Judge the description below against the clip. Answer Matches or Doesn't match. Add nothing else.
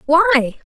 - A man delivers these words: Doesn't match